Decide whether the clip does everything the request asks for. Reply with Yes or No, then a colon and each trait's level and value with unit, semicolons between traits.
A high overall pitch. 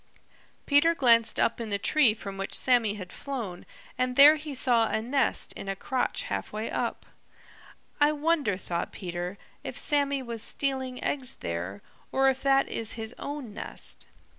Yes: high, 245 Hz